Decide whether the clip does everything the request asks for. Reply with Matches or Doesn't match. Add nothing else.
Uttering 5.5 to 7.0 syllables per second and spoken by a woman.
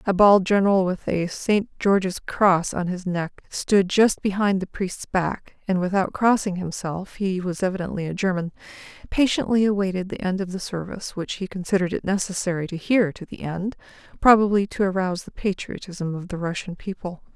Doesn't match